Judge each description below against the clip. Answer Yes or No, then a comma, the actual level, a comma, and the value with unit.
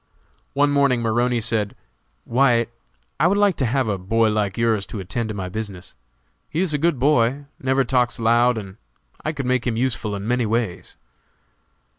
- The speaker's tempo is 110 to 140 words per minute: No, average, 180 wpm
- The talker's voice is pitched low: Yes, low, 120 Hz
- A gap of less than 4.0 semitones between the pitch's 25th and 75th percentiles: Yes, average, 3.5 semitones